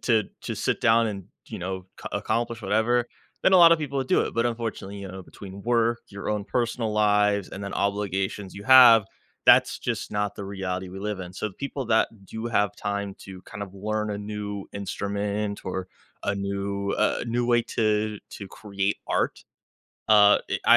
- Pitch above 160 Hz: No, low, 105 Hz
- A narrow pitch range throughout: Yes, narrow, 2.3 semitones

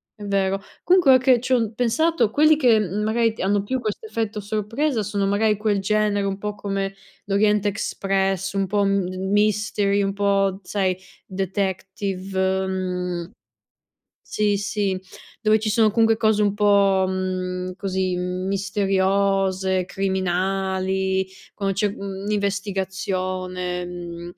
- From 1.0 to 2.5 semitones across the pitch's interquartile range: Yes, narrow, 1.8 semitones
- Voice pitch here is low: No, high, 195 Hz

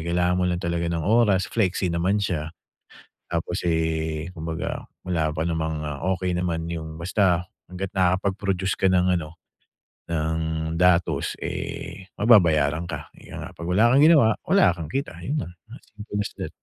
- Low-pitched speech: Yes, very low, 90 Hz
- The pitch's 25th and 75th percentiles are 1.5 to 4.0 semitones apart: Yes, average, 3.0 semitones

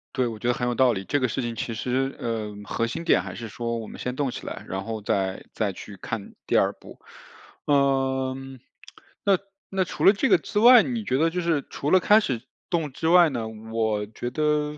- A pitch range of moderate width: No, wide, 6.0 semitones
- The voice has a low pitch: Yes, low, 130 Hz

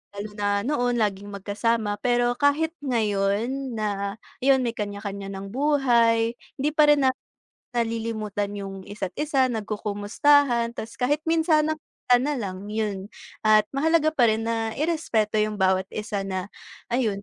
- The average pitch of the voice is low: No, high, 225 Hz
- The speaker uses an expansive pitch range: No, average, 4.6 semitones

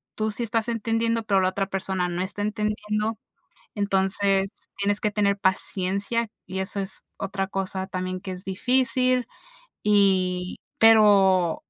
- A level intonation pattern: Yes, narrow, 2.2 semitones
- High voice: Yes, high, 200 Hz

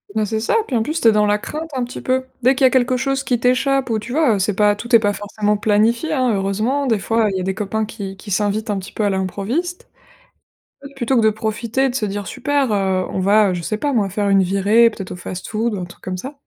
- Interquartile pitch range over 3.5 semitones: Yes, average, 4.0 semitones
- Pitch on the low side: No, high, 220 Hz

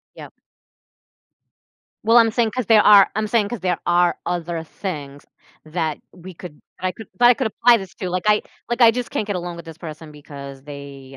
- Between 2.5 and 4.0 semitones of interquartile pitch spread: No, wide, 5.6 semitones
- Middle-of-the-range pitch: Yes, medium, 180 Hz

